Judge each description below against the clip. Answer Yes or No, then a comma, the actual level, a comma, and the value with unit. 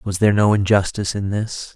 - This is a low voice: Yes, low, 100 Hz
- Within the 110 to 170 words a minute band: No, fast, 205 wpm